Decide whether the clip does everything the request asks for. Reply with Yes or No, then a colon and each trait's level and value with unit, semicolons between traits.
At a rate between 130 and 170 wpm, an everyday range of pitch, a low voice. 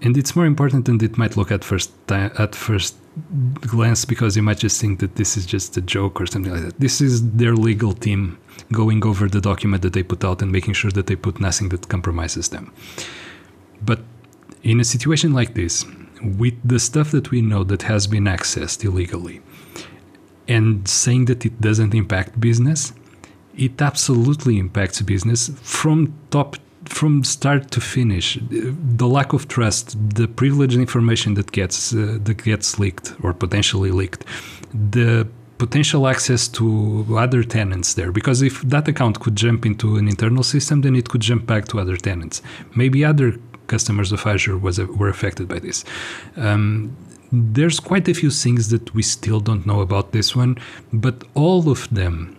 No: average, 180 wpm; average, 3.9 semitones; low, 110 Hz